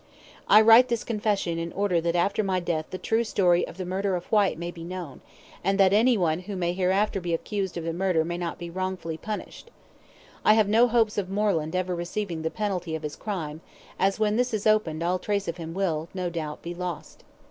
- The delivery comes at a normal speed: No, fast, 225 wpm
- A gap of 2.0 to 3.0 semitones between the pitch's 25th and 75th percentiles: No, average, 3.4 semitones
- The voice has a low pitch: No, medium, 185 Hz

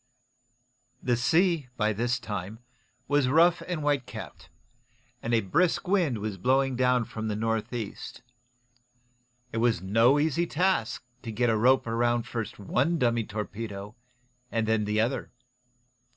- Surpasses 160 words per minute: No, average, 140 wpm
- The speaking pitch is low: Yes, low, 120 Hz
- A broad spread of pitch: No, average, 3.9 semitones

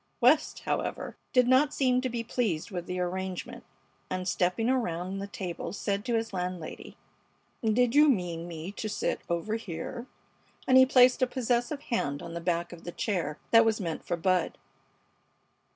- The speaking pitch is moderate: No, high, 200 Hz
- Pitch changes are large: Yes, wide, 5.9 semitones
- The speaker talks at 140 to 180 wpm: Yes, average, 170 wpm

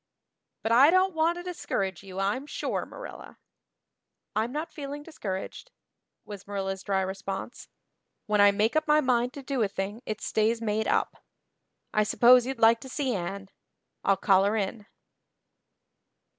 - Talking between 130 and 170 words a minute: Yes, average, 155 wpm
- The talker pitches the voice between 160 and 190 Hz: No, high, 220 Hz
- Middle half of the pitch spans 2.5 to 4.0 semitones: No, average, 5.3 semitones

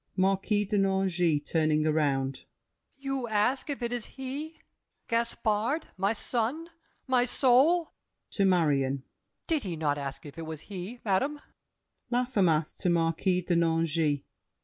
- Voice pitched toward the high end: Yes, high, 195 Hz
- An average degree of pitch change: No, wide, 7.2 semitones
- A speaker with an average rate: No, slow, 125 wpm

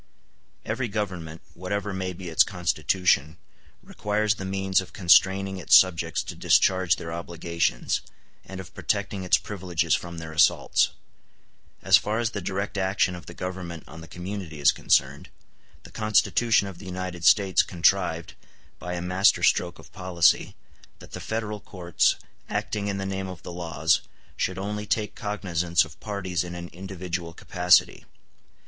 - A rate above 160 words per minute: No, average, 155 wpm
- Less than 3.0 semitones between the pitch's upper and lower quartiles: Yes, narrow, 2.5 semitones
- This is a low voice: Yes, very low, 90 Hz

